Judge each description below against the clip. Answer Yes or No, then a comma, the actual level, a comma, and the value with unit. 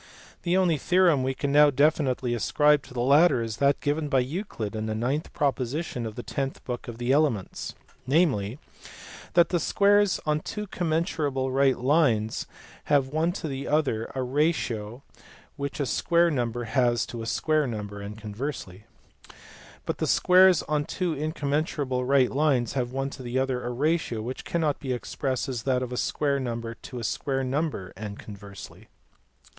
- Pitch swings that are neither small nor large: Yes, average, 4.1 semitones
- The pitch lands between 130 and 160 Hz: Yes, low, 135 Hz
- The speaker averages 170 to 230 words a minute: Yes, average, 175 wpm